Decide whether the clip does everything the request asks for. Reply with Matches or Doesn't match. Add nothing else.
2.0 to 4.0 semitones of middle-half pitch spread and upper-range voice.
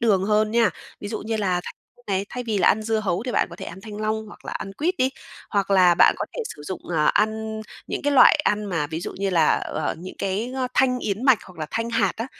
Matches